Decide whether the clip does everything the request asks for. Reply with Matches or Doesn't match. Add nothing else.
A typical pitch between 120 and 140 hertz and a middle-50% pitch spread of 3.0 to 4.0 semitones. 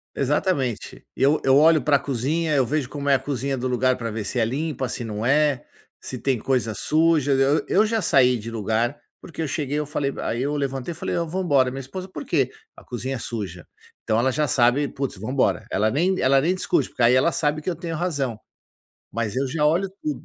Matches